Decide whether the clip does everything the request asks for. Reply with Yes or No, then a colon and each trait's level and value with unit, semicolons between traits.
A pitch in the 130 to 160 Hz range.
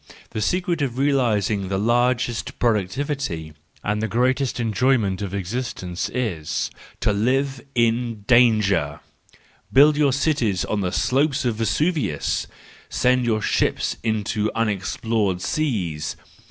No: low, 115 Hz